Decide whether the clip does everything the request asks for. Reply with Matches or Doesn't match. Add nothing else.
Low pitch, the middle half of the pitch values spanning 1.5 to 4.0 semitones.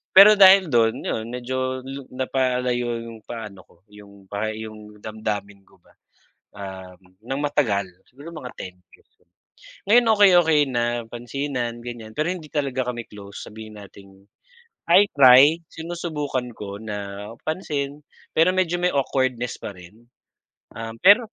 Doesn't match